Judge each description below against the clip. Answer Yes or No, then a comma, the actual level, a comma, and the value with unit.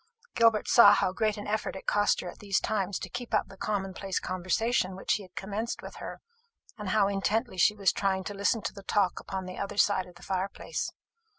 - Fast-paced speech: Yes, fast, 225 wpm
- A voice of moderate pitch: No, high, 200 Hz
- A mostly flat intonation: Yes, narrow, 1.9 semitones